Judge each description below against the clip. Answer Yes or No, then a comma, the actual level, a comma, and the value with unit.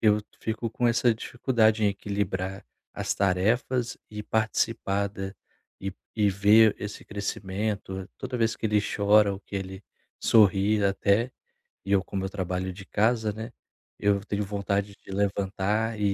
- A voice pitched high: No, low, 100 Hz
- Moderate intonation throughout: No, narrow, 2.1 semitones